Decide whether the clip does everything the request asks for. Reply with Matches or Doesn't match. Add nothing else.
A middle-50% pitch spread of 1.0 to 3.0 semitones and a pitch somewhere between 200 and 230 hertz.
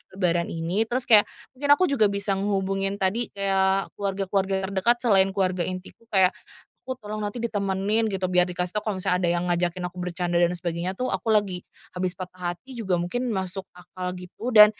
Doesn't match